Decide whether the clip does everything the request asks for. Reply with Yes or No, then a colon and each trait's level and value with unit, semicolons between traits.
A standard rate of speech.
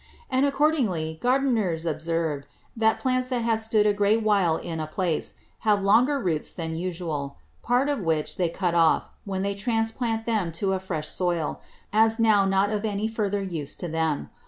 Yes: average, 180 wpm